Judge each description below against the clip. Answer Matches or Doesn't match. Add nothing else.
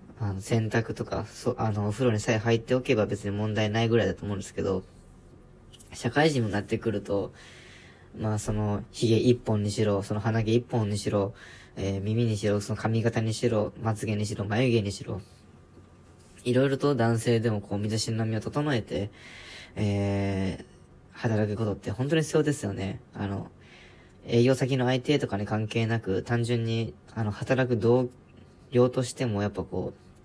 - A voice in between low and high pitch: Doesn't match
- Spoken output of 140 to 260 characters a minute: Doesn't match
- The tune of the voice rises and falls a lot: Doesn't match